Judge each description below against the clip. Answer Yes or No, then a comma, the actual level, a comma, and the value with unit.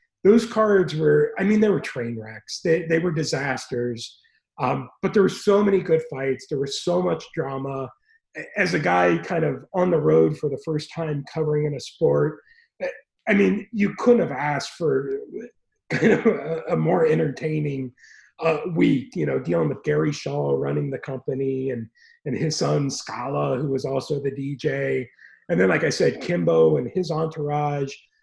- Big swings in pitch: Yes, wide, 6.3 semitones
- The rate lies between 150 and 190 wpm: Yes, average, 180 wpm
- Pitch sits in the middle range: Yes, medium, 150 Hz